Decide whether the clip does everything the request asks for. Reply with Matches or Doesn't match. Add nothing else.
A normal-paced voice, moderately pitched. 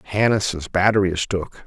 Doesn't match